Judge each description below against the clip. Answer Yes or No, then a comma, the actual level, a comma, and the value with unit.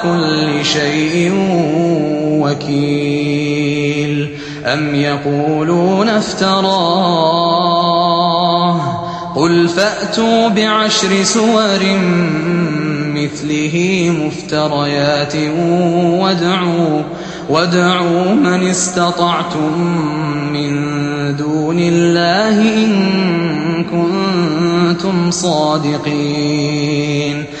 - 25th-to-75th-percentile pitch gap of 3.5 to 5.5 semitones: No, average, 2.9 semitones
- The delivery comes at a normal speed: No, slow, 50 wpm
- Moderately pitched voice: Yes, medium, 170 Hz